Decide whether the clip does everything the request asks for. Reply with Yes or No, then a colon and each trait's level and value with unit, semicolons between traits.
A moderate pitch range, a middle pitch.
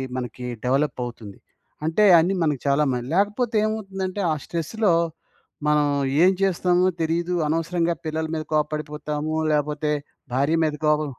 Yes: average, 3.4 semitones; medium, 155 Hz